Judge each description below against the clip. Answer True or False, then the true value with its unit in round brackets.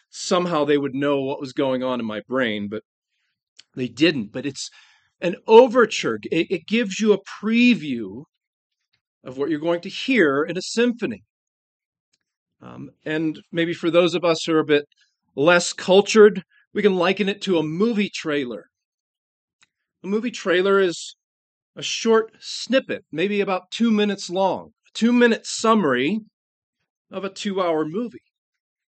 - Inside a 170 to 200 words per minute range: False (155 wpm)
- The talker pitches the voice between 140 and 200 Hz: True (190 Hz)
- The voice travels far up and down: True (6.0 semitones)